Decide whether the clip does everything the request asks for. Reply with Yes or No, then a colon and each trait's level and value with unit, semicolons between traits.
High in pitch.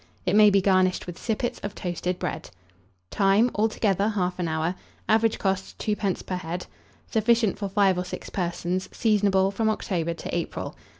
Yes: high, 195 Hz